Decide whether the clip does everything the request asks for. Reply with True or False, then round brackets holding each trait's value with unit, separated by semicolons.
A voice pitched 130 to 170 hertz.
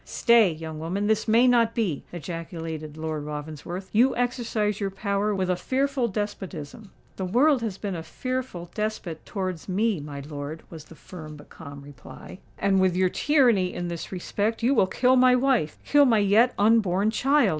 False (195 Hz)